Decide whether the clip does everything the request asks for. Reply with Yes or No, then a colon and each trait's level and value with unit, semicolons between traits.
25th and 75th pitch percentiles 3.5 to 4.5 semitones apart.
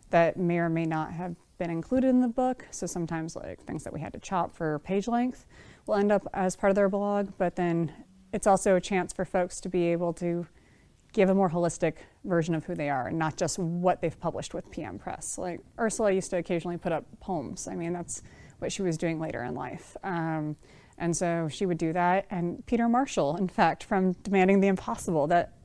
No: average, 2.7 semitones